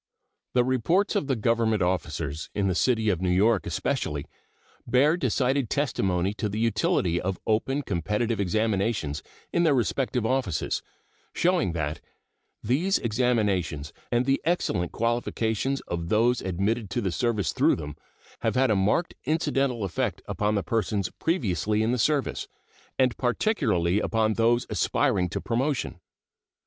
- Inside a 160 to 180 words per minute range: No, average, 140 wpm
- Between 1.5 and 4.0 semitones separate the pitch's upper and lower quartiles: No, average, 5.2 semitones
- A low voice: Yes, low, 110 Hz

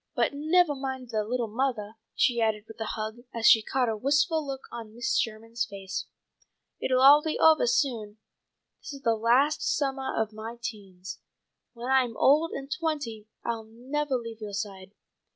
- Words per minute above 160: Yes, average, 170 wpm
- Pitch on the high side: Yes, high, 235 Hz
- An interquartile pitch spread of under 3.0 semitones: No, average, 4.0 semitones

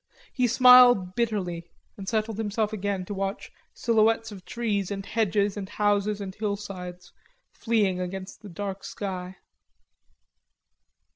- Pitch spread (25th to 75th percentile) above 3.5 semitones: No, narrow, 2.4 semitones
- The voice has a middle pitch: No, high, 205 Hz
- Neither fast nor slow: No, slow, 125 wpm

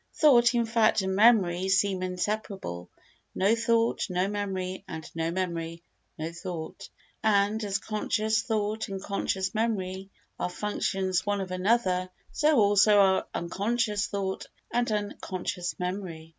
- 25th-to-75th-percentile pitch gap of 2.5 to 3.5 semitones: Yes, average, 2.9 semitones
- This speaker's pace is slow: Yes, slow, 130 wpm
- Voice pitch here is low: No, high, 195 Hz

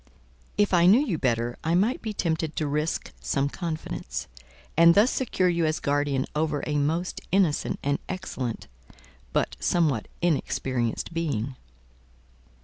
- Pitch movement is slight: No, average, 3.7 semitones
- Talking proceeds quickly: No, average, 140 wpm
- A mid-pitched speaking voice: Yes, medium, 160 Hz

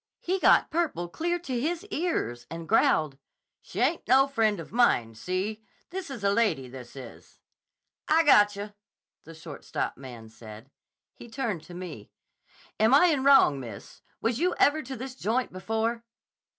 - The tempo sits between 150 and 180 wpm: Yes, average, 160 wpm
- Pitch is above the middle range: Yes, high, 215 Hz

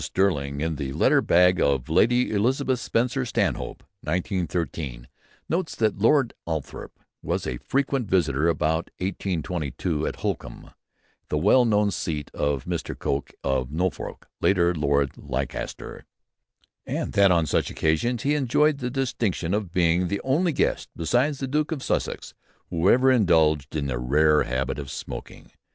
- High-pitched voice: No, very low, 90 Hz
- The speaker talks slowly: No, average, 145 wpm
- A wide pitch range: Yes, wide, 8.3 semitones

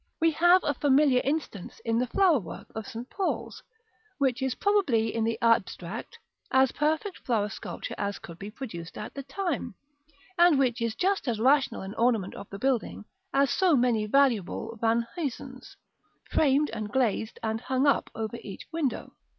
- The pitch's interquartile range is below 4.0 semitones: No, average, 4.5 semitones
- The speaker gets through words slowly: No, average, 170 wpm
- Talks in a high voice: Yes, very high, 250 Hz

